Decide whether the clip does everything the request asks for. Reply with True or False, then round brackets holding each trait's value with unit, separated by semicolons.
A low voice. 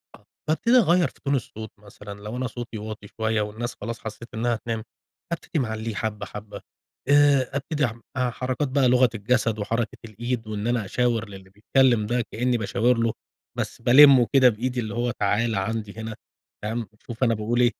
True (115 Hz)